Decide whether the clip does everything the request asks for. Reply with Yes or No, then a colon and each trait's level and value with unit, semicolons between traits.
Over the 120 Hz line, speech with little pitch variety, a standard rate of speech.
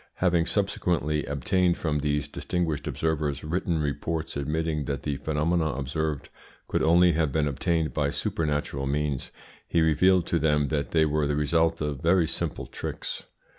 No: very low, 75 Hz; narrow, 2.2 semitones; average, 155 wpm